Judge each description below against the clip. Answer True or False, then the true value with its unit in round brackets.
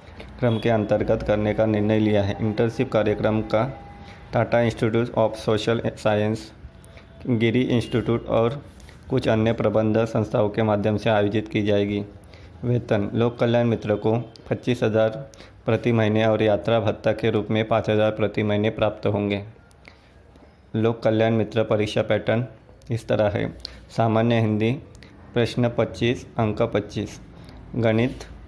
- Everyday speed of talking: True (135 wpm)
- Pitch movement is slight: True (1.8 semitones)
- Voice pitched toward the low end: True (110 Hz)